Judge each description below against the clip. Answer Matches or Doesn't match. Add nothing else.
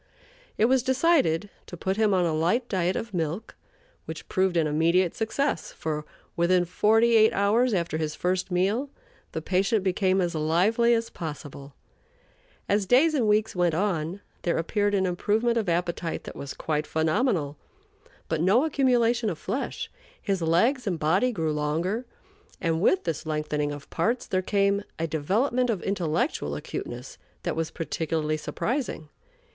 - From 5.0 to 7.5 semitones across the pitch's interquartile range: Matches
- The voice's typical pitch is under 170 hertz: Doesn't match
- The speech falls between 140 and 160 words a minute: Matches